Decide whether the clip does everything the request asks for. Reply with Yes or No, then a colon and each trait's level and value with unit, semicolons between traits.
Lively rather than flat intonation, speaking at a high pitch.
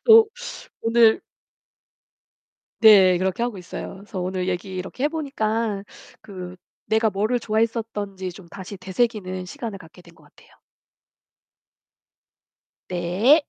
No: average, 3.7 semitones; high, 205 Hz